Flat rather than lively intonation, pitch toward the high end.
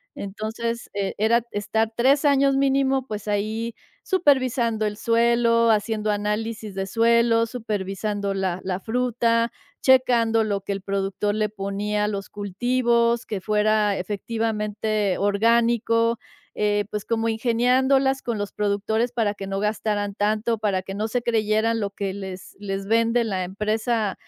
Yes: narrow, 2.3 semitones; high, 220 Hz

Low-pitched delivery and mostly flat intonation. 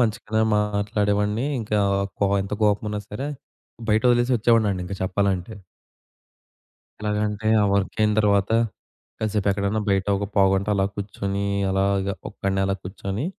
Yes: low, 105 Hz; narrow, 1.5 semitones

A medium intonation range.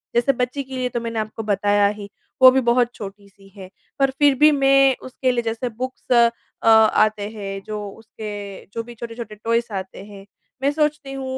Yes: average, 3.8 semitones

